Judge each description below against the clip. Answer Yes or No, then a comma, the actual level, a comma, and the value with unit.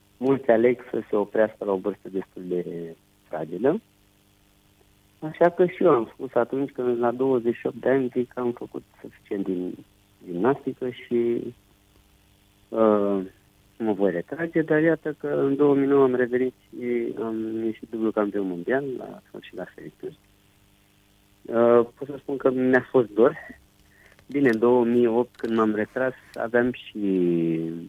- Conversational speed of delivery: Yes, average, 145 wpm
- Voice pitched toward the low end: Yes, low, 110 Hz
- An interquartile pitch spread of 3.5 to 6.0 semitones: Yes, average, 4.0 semitones